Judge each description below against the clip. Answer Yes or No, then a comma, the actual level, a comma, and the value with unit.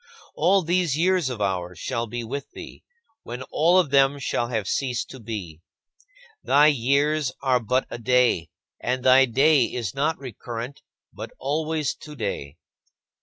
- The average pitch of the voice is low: Yes, low, 130 Hz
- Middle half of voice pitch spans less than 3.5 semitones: No, average, 4.2 semitones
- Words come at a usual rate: Yes, average, 150 wpm